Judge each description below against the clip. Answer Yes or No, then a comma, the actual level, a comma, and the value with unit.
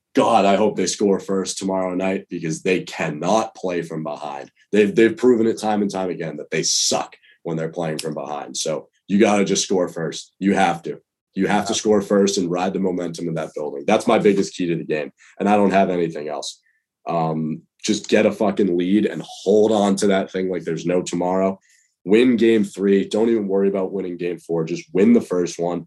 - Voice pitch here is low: Yes, very low, 95 Hz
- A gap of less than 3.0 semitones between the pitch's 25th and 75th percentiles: Yes, narrow, 2.6 semitones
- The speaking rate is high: Yes, fast, 225 wpm